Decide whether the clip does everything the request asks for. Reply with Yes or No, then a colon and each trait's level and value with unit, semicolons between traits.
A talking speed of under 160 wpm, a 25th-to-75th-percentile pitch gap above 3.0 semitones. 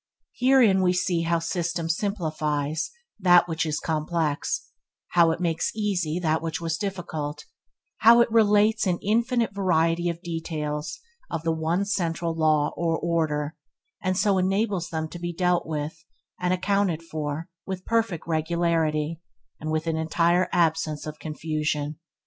No: average, 145 wpm; average, 2.7 semitones